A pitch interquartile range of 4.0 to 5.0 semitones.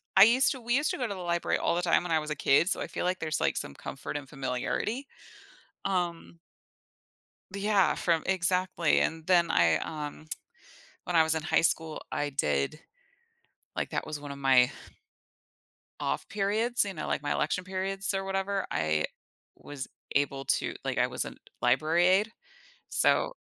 Yes: average, 4.7 semitones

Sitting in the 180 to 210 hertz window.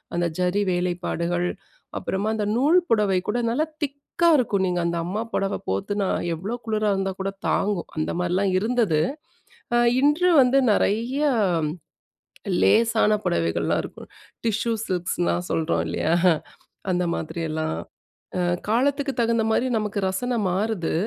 Yes: high, 200 Hz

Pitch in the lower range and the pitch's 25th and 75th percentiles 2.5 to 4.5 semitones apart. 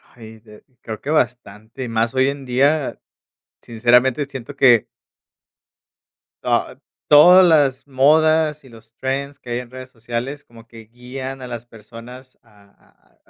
Yes: low, 125 Hz; average, 3.2 semitones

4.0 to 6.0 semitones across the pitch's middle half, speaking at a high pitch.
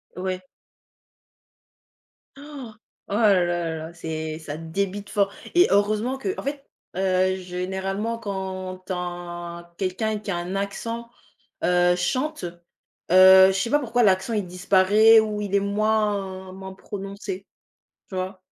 No: average, 2.9 semitones; high, 195 Hz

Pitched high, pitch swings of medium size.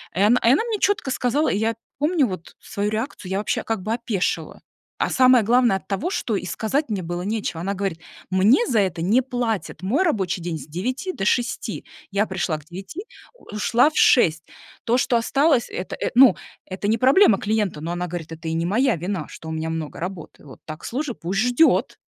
No: high, 210 Hz; wide, 5.8 semitones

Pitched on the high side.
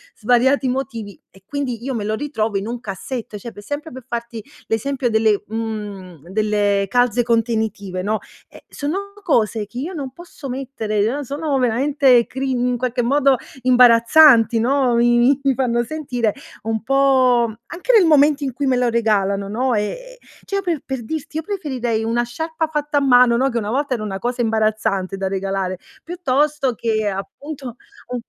Yes: high, 245 Hz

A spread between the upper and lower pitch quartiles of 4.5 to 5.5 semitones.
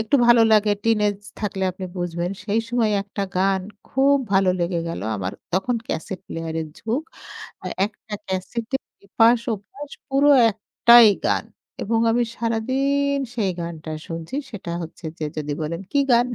Yes: average, 5.0 semitones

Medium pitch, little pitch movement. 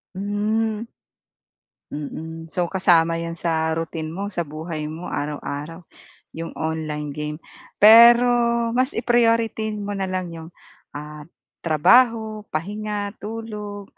No: medium, 180 Hz; average, 5.1 semitones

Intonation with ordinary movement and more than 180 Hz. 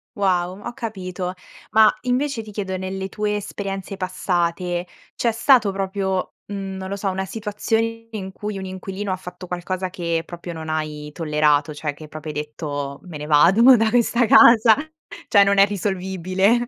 Yes: average, 3.2 semitones; high, 190 Hz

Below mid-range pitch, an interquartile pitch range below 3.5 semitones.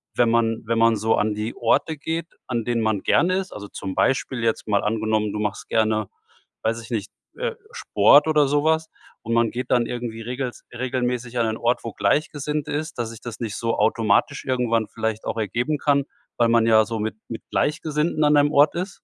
No: low, 115 Hz; average, 4.3 semitones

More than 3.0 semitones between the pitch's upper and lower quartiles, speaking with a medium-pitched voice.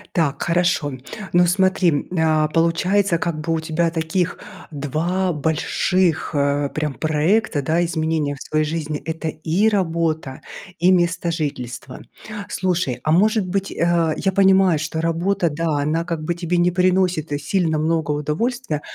No: average, 2.7 semitones; medium, 165 Hz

